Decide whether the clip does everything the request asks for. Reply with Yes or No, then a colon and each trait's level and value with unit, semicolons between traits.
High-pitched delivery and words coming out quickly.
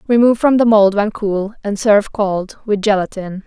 No: high, 210 Hz; average, 190 wpm